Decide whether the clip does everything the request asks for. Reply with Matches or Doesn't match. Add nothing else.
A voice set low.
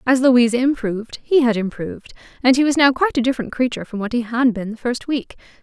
Doesn't match